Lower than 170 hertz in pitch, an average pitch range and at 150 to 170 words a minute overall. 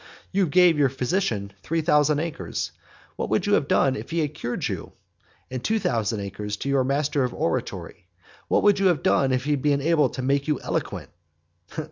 No: medium, 140 Hz; average, 4.2 semitones; average, 195 wpm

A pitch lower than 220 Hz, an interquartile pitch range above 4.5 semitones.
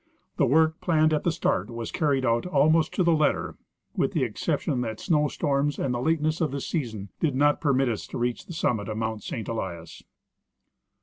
Yes: medium, 140 Hz; average, 5.3 semitones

